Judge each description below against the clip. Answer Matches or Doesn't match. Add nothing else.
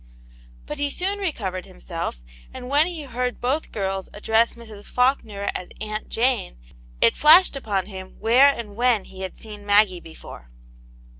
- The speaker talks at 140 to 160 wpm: Matches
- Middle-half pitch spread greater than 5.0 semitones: Matches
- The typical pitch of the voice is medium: Doesn't match